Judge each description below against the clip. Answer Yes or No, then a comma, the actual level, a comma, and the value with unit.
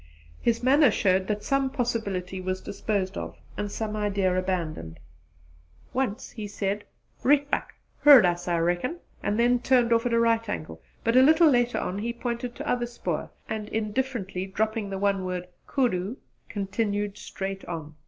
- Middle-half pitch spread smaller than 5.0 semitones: Yes, average, 4.3 semitones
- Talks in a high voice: Yes, high, 210 Hz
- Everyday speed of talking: Yes, average, 165 wpm